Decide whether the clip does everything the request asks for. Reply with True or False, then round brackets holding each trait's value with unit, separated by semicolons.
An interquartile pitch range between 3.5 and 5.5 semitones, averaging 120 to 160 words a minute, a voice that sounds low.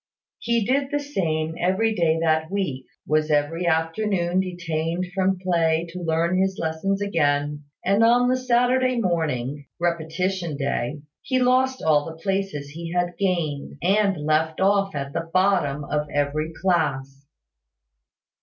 False (4.0 semitones; 140 wpm; 170 Hz)